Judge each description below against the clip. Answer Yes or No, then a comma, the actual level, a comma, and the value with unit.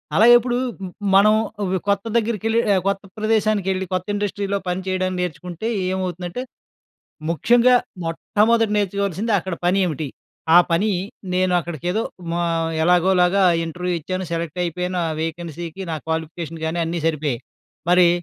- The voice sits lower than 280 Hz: Yes, medium, 185 Hz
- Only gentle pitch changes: No, average, 3.1 semitones